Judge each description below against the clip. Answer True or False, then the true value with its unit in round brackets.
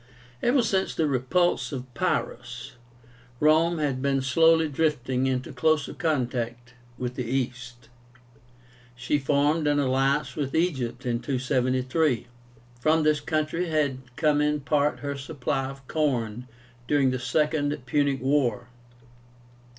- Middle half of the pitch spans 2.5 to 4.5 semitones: True (3.1 semitones)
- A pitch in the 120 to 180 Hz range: True (140 Hz)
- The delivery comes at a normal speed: False (125 wpm)